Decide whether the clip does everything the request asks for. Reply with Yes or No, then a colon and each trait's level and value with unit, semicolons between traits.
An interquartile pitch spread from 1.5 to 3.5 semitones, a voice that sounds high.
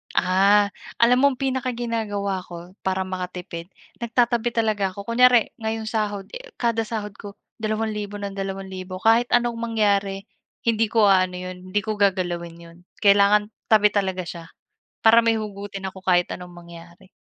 Yes: average, 3.2 semitones; high, 205 Hz